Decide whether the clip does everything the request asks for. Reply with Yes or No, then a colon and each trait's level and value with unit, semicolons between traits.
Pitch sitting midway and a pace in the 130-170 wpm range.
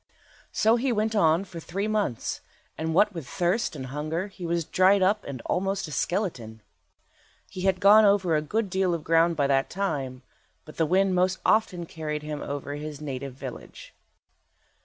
No: medium, 170 Hz; average, 180 wpm